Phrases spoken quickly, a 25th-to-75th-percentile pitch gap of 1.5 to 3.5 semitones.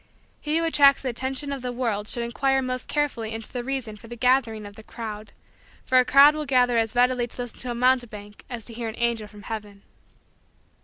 Yes: fast, 220 wpm; average, 2.8 semitones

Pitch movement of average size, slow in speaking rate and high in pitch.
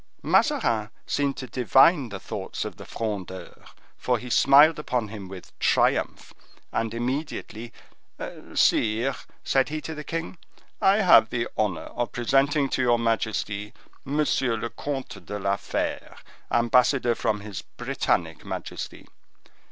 No: average, 4.2 semitones; slow, 130 wpm; low, 120 Hz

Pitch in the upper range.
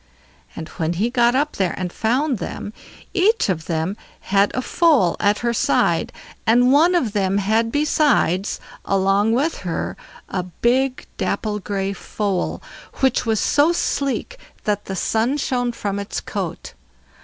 Yes: high, 220 Hz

